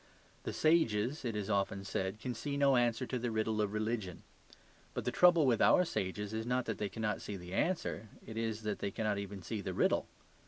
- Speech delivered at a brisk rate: Yes, fast, 220 wpm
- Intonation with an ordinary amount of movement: Yes, average, 3.4 semitones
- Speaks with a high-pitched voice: No, low, 110 Hz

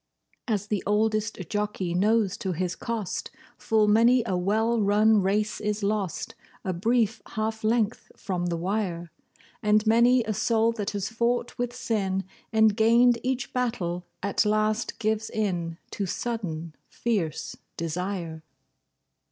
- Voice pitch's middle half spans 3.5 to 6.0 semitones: No, average, 3.0 semitones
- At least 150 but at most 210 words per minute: No, slow, 135 wpm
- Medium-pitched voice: No, high, 210 Hz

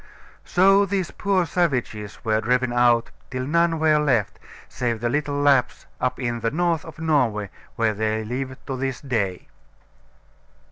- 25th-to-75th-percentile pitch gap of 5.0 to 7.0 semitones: Yes, average, 5.3 semitones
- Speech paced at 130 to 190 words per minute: Yes, average, 150 wpm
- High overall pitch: No, low, 130 Hz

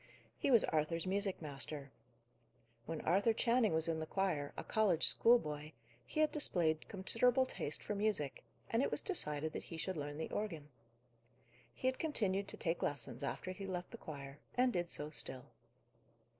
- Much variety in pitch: Yes, wide, 6.0 semitones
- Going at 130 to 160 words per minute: No, average, 170 wpm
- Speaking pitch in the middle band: Yes, medium, 175 Hz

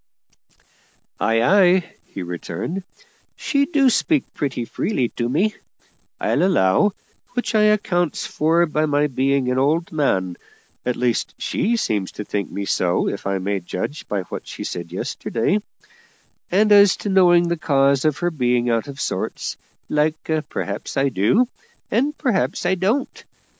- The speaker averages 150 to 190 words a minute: Yes, average, 155 wpm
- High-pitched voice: No, medium, 150 Hz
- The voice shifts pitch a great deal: Yes, wide, 8.4 semitones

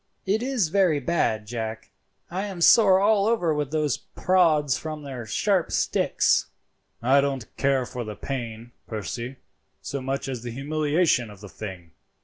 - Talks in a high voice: No, medium, 140 Hz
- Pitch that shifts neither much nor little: No, wide, 6.6 semitones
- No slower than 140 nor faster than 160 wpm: Yes, average, 155 wpm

